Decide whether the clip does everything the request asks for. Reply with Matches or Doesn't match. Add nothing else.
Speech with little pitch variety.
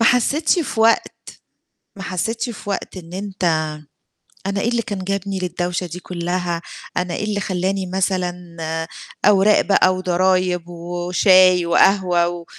Matches